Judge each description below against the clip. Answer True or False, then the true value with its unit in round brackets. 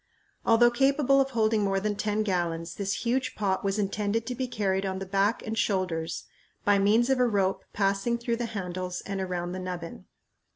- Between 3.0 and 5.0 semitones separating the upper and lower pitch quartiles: True (3.6 semitones)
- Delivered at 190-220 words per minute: True (195 wpm)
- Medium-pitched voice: False (200 Hz)